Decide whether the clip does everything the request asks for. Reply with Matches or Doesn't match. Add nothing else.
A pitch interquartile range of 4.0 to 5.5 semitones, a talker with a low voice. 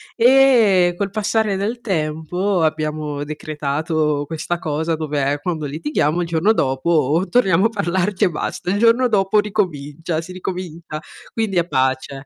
Doesn't match